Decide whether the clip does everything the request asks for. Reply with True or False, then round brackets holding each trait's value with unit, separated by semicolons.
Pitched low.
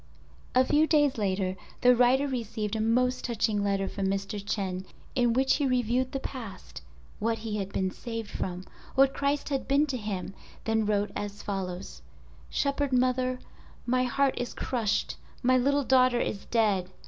False (235 Hz)